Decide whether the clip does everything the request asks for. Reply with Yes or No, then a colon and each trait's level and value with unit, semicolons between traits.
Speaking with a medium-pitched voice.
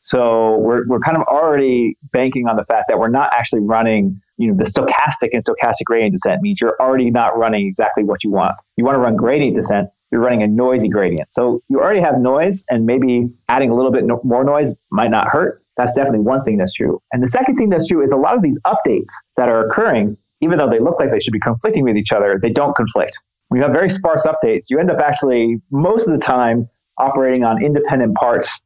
No: low, 125 Hz